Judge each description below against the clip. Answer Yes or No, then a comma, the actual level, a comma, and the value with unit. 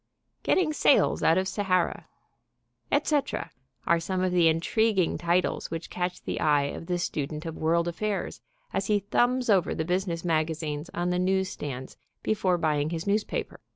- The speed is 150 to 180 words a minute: Yes, average, 160 wpm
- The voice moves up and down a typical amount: Yes, average, 3.1 semitones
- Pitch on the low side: No, medium, 175 Hz